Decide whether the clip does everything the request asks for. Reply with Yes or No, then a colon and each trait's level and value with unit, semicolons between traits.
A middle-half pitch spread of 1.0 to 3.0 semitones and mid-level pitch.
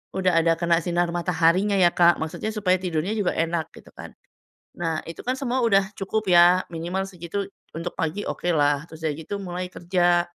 Yes: narrow, 2.5 semitones; medium, 175 Hz